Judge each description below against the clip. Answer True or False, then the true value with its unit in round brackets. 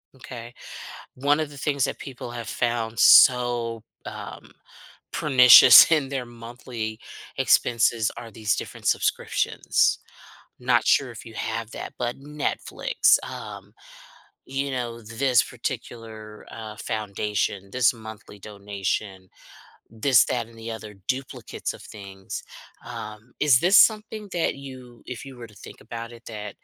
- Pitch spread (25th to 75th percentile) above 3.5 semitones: False (2.8 semitones)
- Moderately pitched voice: False (120 Hz)